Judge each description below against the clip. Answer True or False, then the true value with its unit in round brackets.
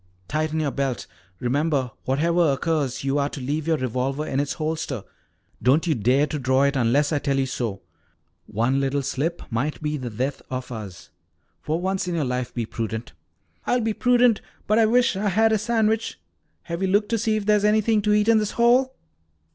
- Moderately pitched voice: True (150 Hz)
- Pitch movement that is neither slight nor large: False (8.0 semitones)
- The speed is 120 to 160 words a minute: False (200 wpm)